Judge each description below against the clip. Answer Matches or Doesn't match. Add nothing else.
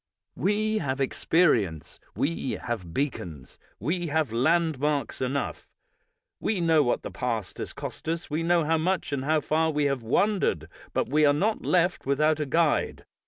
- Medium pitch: Matches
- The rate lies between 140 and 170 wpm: Matches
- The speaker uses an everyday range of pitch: Matches